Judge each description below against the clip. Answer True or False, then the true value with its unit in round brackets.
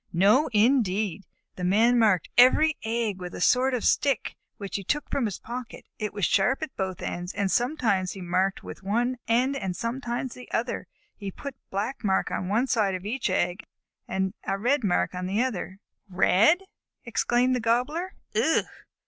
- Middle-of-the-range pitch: False (220 Hz)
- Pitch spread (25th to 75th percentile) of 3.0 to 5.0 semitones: True (4.7 semitones)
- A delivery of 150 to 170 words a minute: False (185 wpm)